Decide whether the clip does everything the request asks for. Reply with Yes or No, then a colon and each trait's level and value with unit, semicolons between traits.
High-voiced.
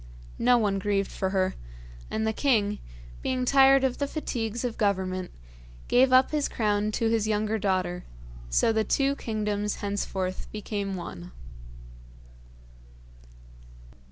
Yes: high, 215 Hz